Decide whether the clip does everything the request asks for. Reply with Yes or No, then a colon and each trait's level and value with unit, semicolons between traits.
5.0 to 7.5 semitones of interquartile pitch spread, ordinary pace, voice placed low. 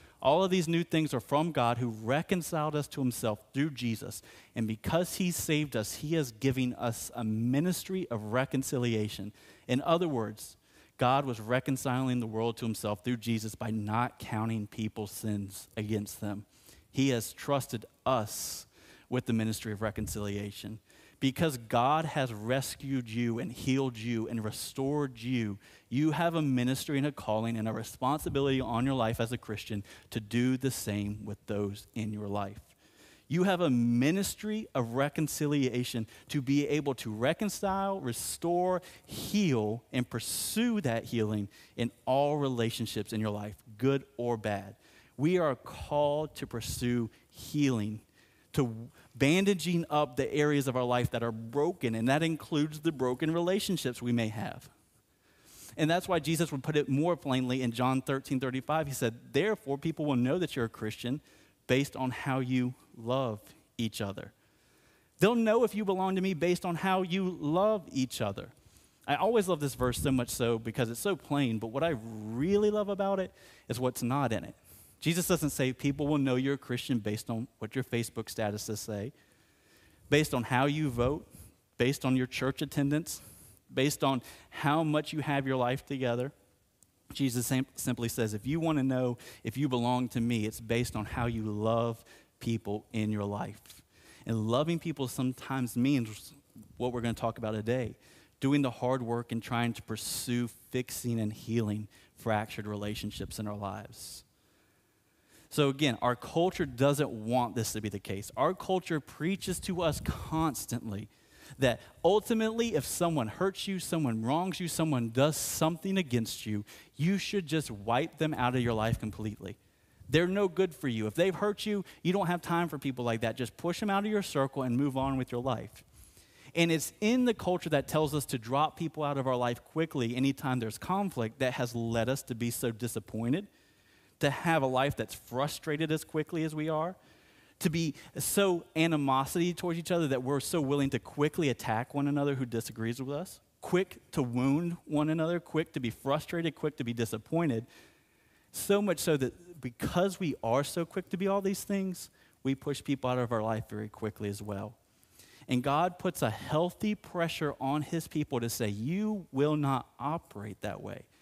Yes: average, 5.3 semitones; average, 180 wpm; low, 130 Hz